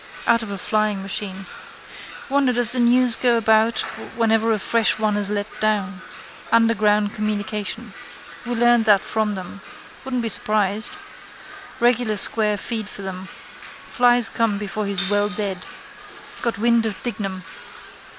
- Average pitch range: No, narrow, 2.2 semitones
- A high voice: Yes, high, 215 Hz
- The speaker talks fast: No, average, 140 wpm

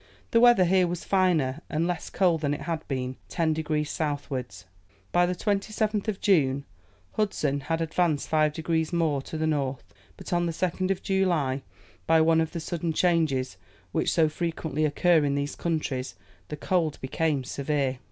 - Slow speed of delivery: No, average, 170 wpm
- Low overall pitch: No, medium, 160 Hz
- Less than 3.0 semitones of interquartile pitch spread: No, average, 3.5 semitones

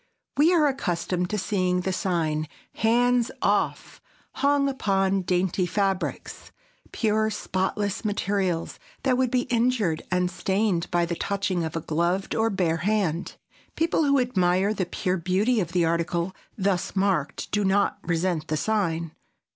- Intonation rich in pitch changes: No, average, 3.7 semitones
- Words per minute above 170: No, average, 140 wpm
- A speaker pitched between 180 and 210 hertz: Yes, high, 190 Hz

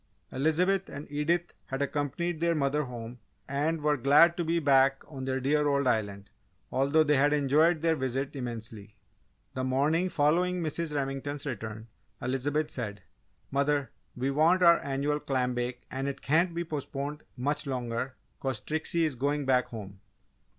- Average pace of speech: Yes, average, 155 wpm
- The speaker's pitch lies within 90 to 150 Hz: Yes, medium, 140 Hz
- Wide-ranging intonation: No, average, 3.0 semitones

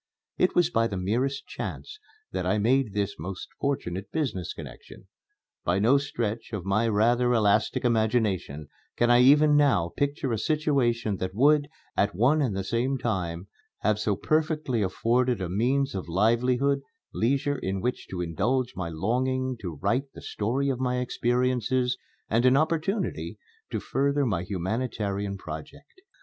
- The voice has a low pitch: Yes, low, 120 Hz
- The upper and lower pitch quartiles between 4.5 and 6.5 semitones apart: Yes, average, 5.3 semitones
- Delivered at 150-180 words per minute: Yes, average, 155 wpm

